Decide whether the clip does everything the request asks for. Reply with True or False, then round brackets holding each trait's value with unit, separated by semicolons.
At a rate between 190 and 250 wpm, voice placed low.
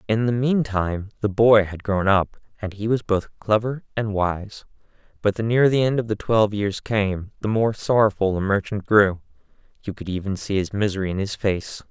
True (200 wpm; 105 Hz)